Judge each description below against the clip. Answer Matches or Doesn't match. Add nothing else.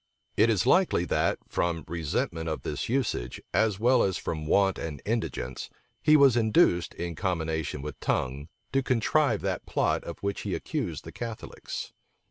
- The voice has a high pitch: Doesn't match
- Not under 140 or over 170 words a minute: Matches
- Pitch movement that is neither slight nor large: Doesn't match